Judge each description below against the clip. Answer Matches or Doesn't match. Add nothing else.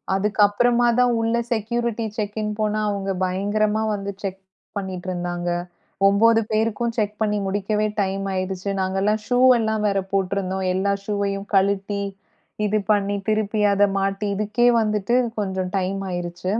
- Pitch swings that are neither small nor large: Doesn't match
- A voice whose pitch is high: Matches